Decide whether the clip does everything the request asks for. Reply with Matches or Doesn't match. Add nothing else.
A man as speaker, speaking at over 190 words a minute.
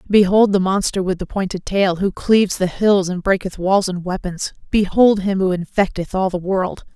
Doesn't match